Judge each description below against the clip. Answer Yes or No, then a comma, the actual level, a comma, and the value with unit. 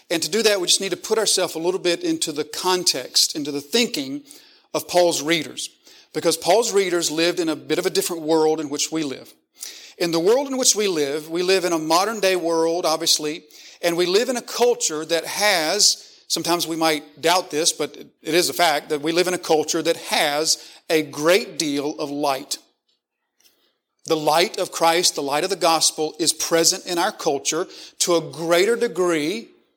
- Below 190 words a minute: No, fast, 205 wpm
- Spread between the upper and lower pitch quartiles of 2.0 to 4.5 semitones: Yes, average, 2.9 semitones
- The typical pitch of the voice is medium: Yes, medium, 165 Hz